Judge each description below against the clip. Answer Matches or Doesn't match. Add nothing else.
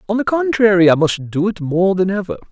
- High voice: Matches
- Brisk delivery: Matches